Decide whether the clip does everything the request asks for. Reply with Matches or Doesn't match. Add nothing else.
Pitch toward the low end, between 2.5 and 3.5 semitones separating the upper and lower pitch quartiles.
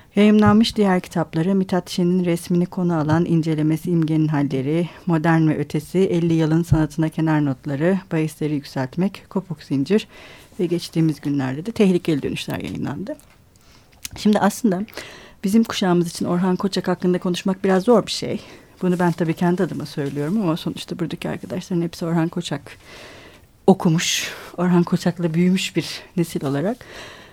Doesn't match